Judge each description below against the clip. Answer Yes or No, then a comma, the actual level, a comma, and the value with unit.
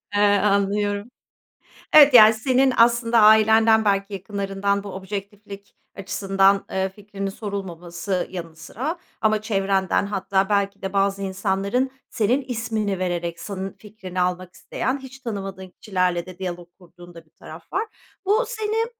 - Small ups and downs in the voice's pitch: Yes, narrow, 2.3 semitones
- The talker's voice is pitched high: Yes, high, 200 Hz